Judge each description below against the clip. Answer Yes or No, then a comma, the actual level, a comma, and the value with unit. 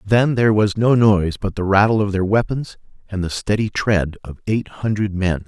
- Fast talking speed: Yes, fast, 210 wpm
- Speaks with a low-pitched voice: Yes, low, 100 Hz